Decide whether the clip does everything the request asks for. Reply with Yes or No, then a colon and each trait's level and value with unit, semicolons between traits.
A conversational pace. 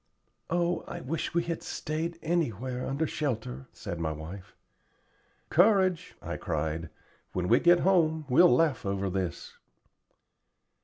No: slow, 125 wpm